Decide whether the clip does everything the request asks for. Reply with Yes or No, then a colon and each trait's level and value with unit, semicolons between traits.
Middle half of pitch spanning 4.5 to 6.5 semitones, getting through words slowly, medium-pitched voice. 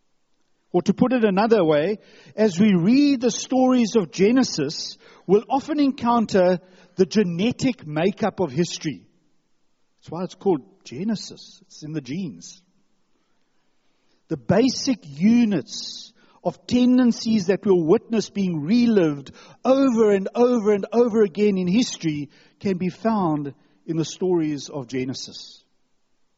No: average, 5.0 semitones; slow, 125 wpm; high, 205 Hz